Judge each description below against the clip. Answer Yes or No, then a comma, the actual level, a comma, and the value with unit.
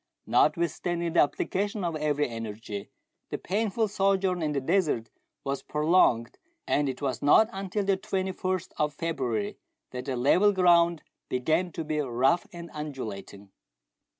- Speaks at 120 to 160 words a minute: Yes, average, 140 wpm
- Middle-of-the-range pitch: Yes, medium, 160 Hz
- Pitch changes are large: Yes, wide, 5.9 semitones